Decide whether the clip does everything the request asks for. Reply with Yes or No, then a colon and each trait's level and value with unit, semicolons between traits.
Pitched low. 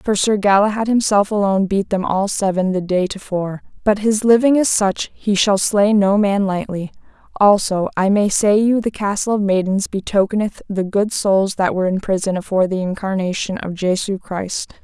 No: high, 200 Hz